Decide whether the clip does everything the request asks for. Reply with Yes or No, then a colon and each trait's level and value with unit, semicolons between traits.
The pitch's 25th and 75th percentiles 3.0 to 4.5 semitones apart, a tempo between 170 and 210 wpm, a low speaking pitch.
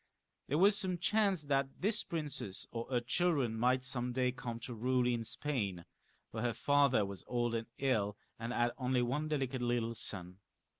Yes: average, 3.6 semitones; average, 180 wpm; low, 125 Hz